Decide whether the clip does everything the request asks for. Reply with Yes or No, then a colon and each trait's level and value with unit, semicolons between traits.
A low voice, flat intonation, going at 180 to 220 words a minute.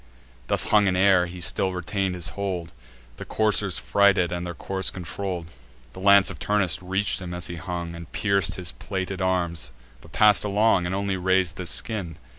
Yes: very low, 95 Hz; narrow, 2.1 semitones; average, 185 wpm